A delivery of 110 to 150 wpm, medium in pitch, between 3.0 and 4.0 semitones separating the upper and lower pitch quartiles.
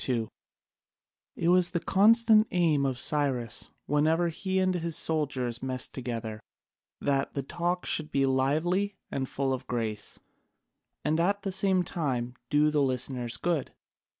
No: average, 145 wpm; medium, 150 Hz; average, 5.2 semitones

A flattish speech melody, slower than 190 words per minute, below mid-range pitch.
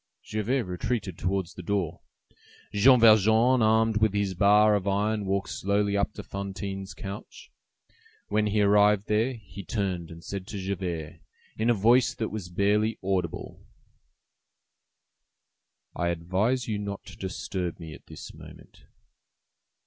Yes: narrow, 2.3 semitones; average, 140 wpm; low, 100 Hz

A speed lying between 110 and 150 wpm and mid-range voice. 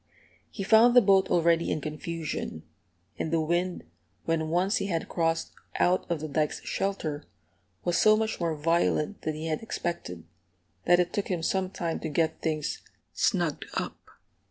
No: average, 165 wpm; medium, 170 Hz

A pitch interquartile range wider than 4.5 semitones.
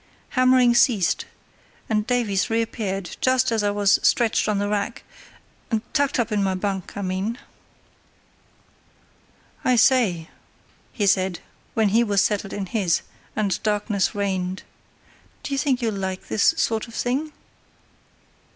No: average, 3.5 semitones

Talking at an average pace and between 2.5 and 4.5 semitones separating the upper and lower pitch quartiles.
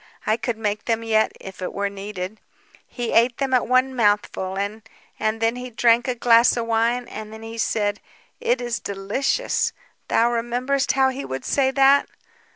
Yes: average, 180 wpm; average, 2.8 semitones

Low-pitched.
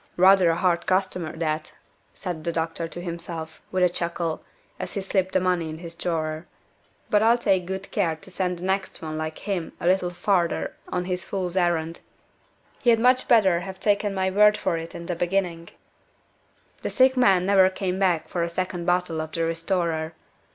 No: medium, 180 Hz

